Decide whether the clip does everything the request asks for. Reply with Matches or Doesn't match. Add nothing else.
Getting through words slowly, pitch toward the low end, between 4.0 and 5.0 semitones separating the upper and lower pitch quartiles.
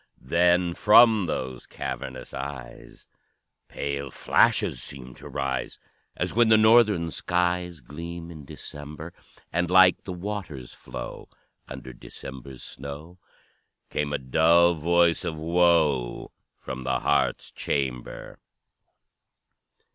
Matches